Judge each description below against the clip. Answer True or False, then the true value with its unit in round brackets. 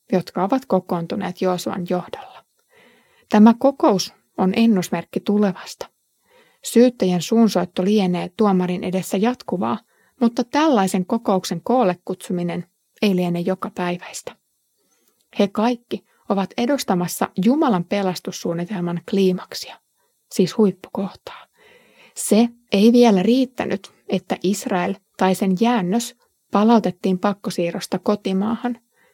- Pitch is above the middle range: True (200 Hz)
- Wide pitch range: False (4.2 semitones)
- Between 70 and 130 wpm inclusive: True (95 wpm)